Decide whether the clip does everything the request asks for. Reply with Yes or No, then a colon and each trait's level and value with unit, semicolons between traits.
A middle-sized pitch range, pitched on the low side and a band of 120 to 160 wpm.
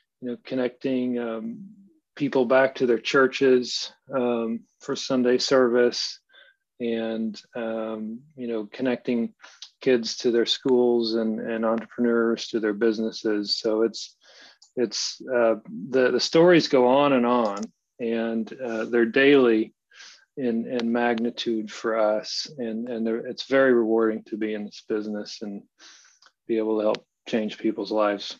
No: narrow, 2.1 semitones; low, 115 Hz; average, 140 wpm